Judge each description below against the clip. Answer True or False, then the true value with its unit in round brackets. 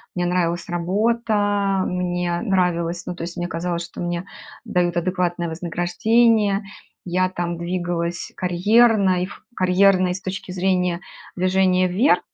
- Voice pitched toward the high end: False (180 Hz)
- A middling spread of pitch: False (1.8 semitones)